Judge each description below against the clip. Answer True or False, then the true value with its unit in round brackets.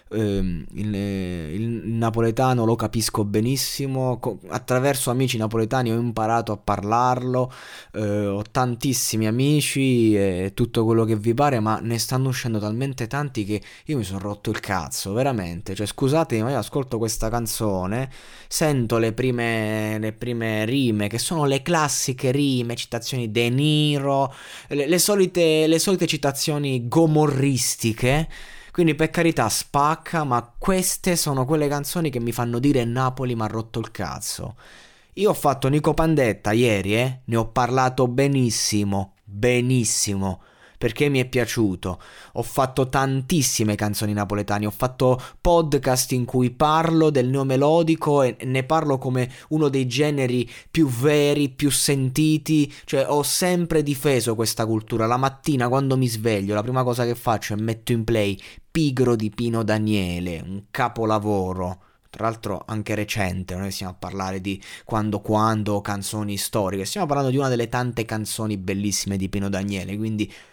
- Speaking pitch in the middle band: False (120 Hz)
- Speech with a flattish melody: False (4.3 semitones)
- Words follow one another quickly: False (150 wpm)